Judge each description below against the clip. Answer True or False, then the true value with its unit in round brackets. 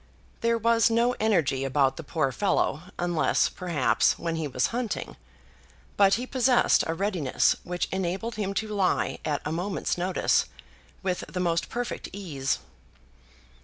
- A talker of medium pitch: True (180 Hz)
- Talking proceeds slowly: False (145 wpm)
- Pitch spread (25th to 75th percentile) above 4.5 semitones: True (5.3 semitones)